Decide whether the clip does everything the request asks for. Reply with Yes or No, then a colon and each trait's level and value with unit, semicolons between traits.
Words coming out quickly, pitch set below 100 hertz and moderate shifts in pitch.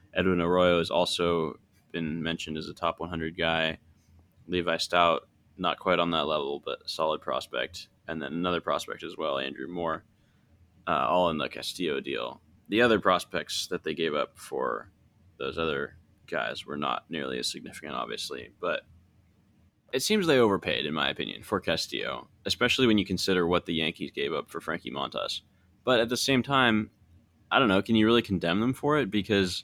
No: average, 185 wpm; very low, 90 Hz; average, 4.2 semitones